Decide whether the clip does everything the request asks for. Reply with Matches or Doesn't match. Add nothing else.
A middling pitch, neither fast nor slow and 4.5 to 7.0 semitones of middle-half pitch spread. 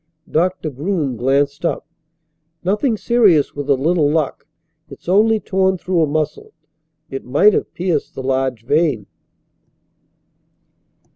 Doesn't match